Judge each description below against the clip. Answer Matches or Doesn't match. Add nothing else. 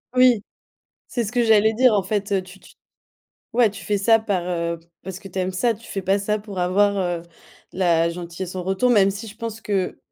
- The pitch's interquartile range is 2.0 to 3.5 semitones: Matches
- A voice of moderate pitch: Doesn't match